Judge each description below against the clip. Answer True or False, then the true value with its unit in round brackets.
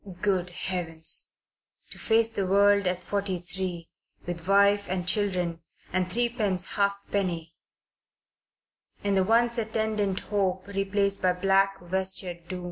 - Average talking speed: False (125 wpm)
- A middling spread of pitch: False (1.9 semitones)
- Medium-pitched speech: False (195 Hz)